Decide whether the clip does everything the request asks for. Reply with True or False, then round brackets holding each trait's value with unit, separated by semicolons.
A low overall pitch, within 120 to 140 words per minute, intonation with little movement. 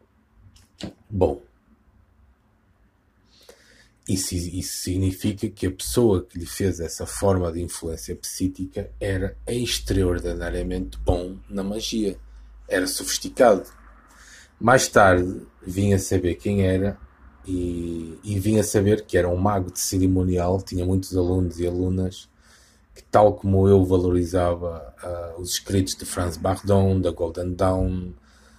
True (95 Hz; 125 wpm; 2.0 semitones)